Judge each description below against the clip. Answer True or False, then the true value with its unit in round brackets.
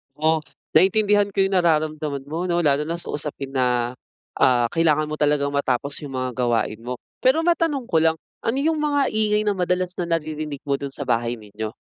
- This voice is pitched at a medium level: True (155 Hz)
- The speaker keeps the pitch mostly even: False (5.4 semitones)